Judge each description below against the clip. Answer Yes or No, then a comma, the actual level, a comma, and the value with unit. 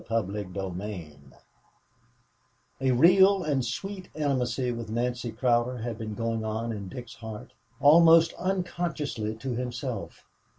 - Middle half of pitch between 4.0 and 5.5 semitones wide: Yes, average, 4.8 semitones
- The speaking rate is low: Yes, slow, 120 wpm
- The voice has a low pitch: Yes, low, 120 Hz